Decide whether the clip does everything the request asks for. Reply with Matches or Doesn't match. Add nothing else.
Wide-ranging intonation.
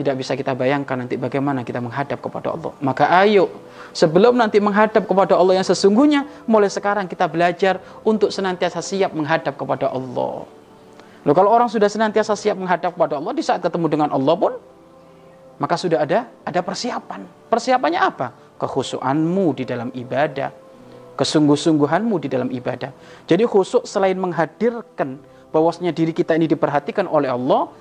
Matches